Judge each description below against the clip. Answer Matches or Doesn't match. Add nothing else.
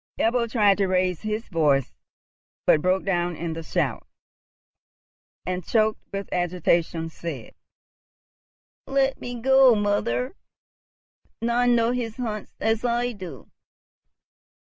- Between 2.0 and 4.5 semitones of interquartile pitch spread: Doesn't match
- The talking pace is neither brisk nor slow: Doesn't match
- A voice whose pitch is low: Doesn't match